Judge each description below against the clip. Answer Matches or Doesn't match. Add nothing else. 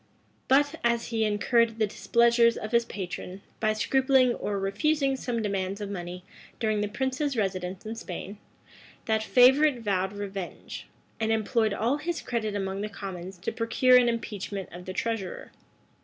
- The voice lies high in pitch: Matches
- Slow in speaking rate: Doesn't match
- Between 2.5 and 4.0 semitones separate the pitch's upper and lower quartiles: Matches